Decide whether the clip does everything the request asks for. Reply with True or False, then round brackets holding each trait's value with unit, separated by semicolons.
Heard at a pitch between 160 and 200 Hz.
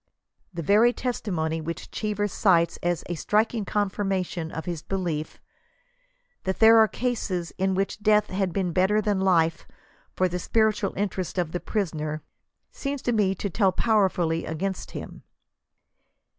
True (190 Hz)